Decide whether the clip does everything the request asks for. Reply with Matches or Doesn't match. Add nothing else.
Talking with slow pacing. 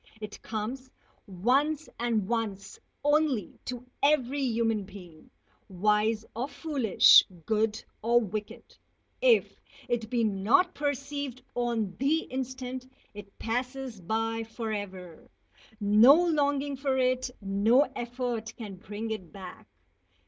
Matches